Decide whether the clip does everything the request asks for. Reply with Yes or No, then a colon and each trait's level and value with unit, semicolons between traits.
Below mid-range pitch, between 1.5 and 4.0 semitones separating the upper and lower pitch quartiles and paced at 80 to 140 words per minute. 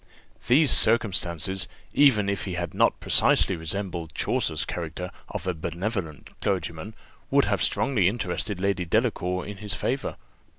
Yes: very low, 95 Hz; average, 3.6 semitones; slow, 135 wpm